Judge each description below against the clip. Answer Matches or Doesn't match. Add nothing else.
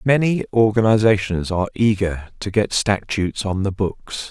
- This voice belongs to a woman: Doesn't match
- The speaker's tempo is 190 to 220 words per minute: Doesn't match